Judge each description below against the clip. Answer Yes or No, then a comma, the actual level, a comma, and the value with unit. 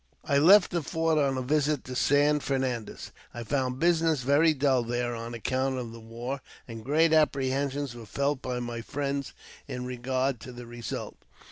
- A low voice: Yes, low, 130 Hz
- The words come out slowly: No, average, 175 wpm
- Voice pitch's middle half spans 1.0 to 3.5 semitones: Yes, average, 3.0 semitones